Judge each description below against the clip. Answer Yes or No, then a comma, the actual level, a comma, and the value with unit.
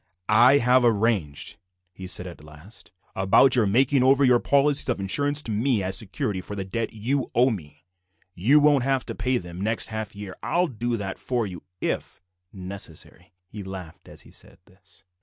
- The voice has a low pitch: Yes, low, 110 Hz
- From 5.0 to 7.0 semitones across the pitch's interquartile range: Yes, average, 5.3 semitones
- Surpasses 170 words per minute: Yes, average, 185 wpm